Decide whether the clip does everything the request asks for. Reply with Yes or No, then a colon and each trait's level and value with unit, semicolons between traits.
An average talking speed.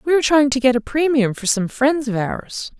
No: fast, 260 wpm